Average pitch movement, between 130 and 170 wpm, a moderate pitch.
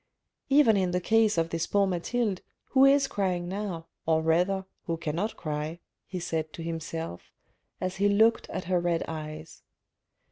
Yes: average, 3.7 semitones; average, 165 wpm; medium, 180 Hz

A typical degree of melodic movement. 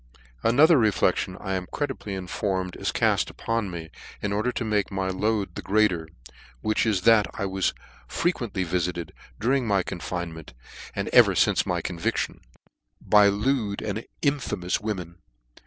Yes: average, 3.4 semitones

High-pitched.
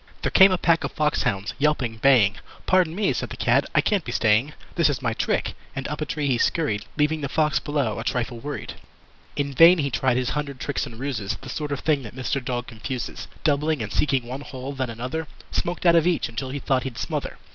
No: medium, 140 Hz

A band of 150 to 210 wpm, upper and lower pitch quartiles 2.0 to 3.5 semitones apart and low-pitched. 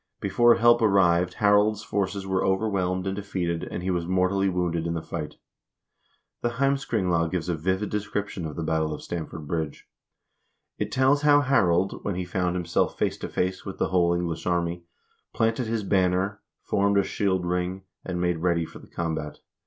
Yes: average, 175 wpm; average, 2.9 semitones; very low, 90 Hz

